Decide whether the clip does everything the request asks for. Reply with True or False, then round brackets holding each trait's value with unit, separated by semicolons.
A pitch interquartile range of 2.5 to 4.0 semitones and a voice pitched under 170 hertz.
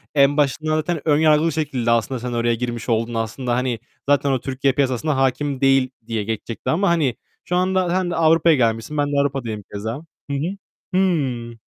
False (4.6 semitones; 135 Hz)